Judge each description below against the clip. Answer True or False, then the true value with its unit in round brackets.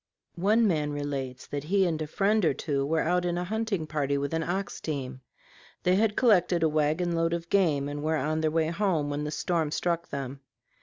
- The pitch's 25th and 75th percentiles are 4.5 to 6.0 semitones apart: False (3.5 semitones)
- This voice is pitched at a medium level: True (160 Hz)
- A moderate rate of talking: False (215 wpm)